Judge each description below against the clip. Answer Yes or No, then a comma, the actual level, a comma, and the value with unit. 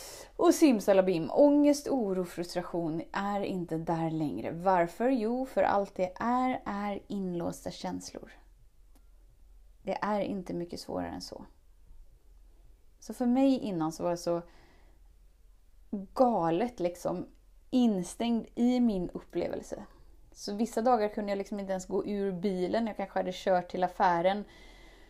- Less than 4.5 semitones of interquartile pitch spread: No, average, 5.3 semitones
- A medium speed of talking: Yes, average, 135 wpm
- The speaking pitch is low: No, high, 190 Hz